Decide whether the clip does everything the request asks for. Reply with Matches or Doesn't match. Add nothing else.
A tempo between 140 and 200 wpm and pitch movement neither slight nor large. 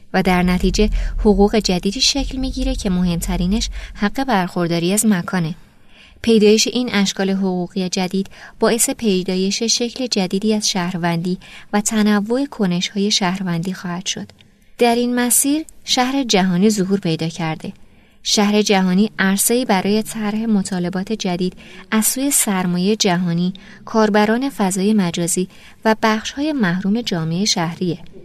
Doesn't match